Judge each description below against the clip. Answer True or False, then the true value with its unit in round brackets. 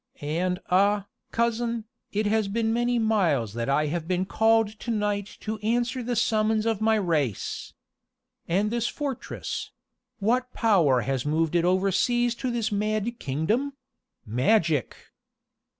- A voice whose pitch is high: True (210 Hz)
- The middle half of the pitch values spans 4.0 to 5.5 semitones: True (5.0 semitones)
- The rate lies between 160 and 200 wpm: False (135 wpm)